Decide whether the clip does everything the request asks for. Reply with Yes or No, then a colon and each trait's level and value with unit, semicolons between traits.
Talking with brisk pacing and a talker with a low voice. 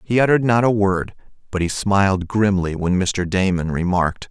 No: average, 180 wpm; low, 100 Hz